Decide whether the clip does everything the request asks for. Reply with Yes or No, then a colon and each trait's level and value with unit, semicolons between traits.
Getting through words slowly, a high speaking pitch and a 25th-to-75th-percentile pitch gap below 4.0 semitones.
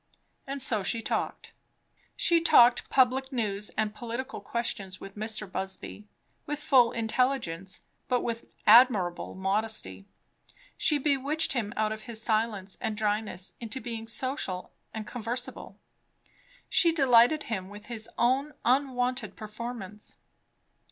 Yes: slow, 125 wpm; high, 230 Hz; average, 3.5 semitones